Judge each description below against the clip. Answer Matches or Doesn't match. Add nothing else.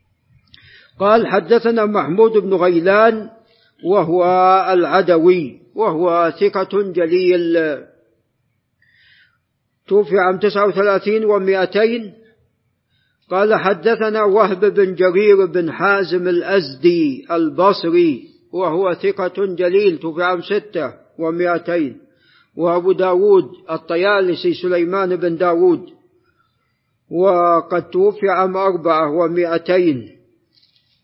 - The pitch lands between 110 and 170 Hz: Doesn't match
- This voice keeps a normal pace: Matches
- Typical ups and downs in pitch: Matches